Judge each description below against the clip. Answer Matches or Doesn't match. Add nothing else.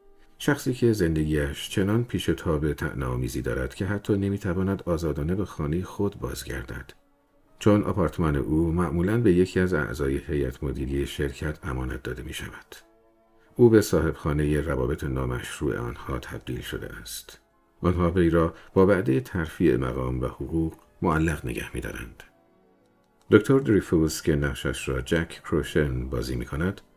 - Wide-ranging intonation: Matches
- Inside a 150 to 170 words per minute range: Doesn't match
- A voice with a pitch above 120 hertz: Doesn't match